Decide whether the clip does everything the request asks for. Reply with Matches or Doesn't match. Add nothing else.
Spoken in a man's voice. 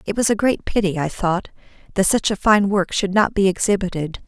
Doesn't match